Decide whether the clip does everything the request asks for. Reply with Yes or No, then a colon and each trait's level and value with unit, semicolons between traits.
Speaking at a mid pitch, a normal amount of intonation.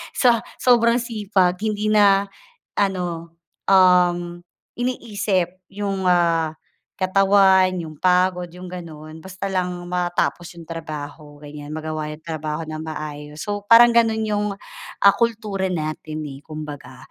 Yes: medium, 180 Hz; average, 4.2 semitones